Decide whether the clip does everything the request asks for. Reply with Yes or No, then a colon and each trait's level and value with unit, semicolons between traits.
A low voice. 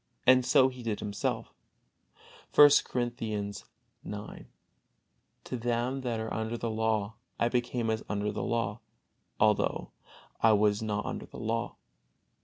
Yes: low, 110 Hz